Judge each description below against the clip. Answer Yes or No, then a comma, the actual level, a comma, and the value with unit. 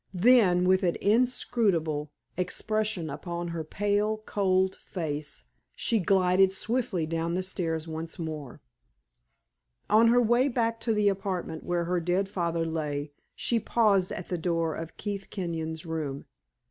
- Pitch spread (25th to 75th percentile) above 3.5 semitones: Yes, average, 4.1 semitones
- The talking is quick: No, average, 140 wpm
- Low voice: No, medium, 180 Hz